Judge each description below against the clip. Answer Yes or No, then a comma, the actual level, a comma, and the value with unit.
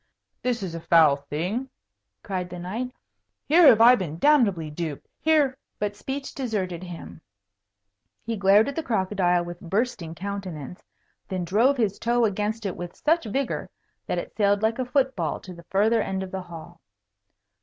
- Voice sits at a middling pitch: No, high, 200 Hz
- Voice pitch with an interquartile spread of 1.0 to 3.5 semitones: No, wide, 5.4 semitones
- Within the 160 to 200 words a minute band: Yes, average, 175 wpm